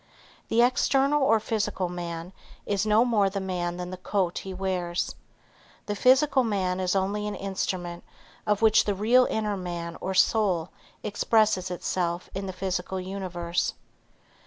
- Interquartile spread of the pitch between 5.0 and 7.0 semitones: No, average, 2.9 semitones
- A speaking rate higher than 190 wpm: No, average, 150 wpm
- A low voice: No, high, 190 Hz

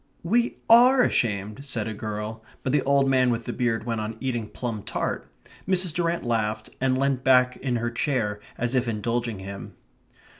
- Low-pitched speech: Yes, low, 120 Hz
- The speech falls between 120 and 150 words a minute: No, average, 180 wpm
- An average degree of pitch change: Yes, average, 3.7 semitones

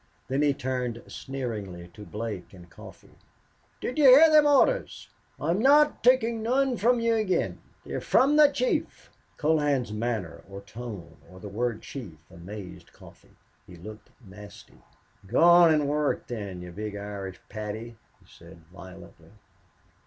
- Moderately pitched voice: No, low, 120 Hz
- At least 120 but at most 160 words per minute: Yes, average, 145 wpm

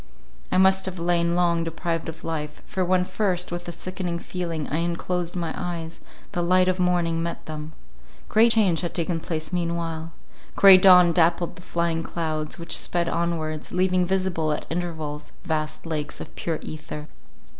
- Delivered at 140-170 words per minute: Yes, average, 165 wpm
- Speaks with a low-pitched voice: No, medium, 170 Hz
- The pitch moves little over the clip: Yes, narrow, 1.7 semitones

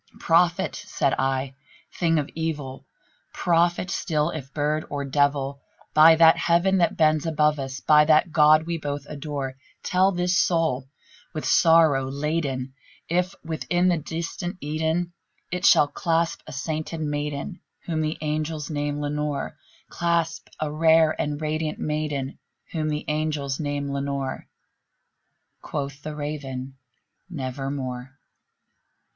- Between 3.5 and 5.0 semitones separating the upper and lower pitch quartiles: No, narrow, 2.5 semitones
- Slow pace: Yes, slow, 130 wpm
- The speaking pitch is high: No, medium, 150 Hz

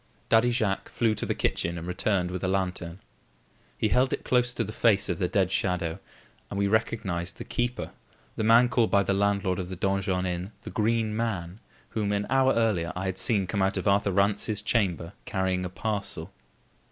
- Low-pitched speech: Yes, low, 100 Hz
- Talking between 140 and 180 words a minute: No, average, 200 wpm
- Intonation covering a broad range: No, average, 3.1 semitones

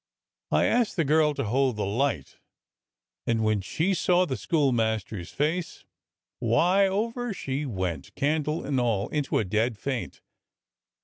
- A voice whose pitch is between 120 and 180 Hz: Yes, low, 135 Hz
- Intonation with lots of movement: Yes, wide, 6.5 semitones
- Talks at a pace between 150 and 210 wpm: No, average, 140 wpm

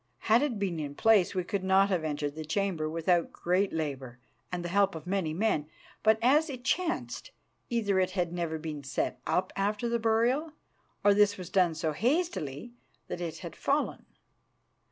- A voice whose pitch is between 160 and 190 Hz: Yes, medium, 185 Hz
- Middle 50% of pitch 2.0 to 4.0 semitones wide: No, wide, 5.5 semitones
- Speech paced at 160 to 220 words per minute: Yes, average, 180 wpm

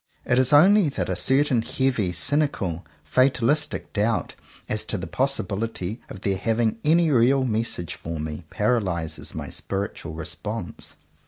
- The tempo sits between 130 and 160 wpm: Yes, average, 140 wpm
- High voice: No, low, 115 Hz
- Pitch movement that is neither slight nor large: No, wide, 6.1 semitones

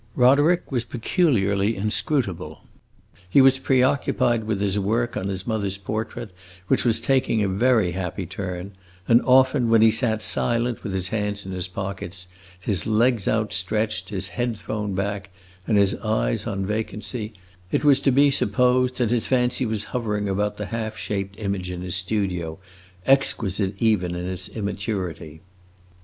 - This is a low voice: Yes, low, 105 Hz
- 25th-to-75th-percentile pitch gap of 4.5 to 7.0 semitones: No, average, 3.6 semitones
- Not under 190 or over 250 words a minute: No, average, 155 wpm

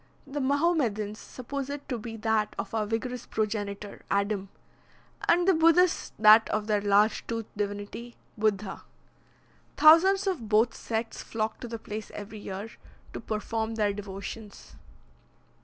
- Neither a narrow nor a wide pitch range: Yes, average, 3.4 semitones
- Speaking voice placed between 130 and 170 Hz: No, high, 220 Hz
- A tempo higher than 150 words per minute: No, average, 140 wpm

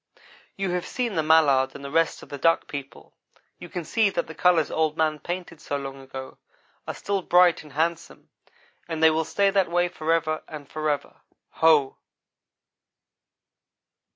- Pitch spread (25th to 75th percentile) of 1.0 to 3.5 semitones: Yes, average, 3.0 semitones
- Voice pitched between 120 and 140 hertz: No, medium, 160 Hz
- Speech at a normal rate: Yes, average, 165 wpm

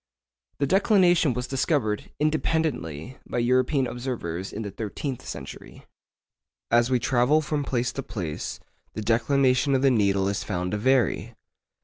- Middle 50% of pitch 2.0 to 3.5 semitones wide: No, average, 4.7 semitones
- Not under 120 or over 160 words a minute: Yes, average, 140 wpm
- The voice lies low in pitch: Yes, low, 125 Hz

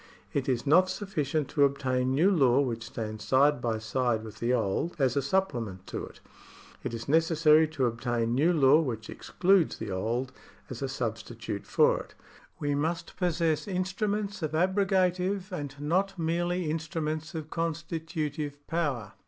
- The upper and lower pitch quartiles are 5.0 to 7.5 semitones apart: Yes, average, 5.3 semitones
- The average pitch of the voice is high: No, medium, 150 Hz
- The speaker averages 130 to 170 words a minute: Yes, average, 160 wpm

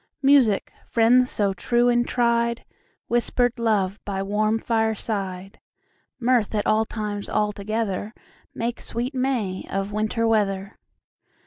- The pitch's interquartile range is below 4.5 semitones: Yes, average, 2.7 semitones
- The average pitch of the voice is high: Yes, high, 220 Hz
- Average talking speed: No, slow, 105 wpm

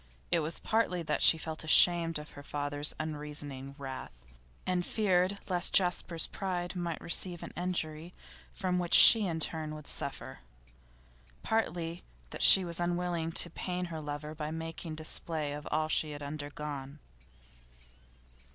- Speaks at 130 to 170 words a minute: Yes, average, 145 wpm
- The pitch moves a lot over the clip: No, average, 2.8 semitones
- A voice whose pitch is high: No, medium, 160 Hz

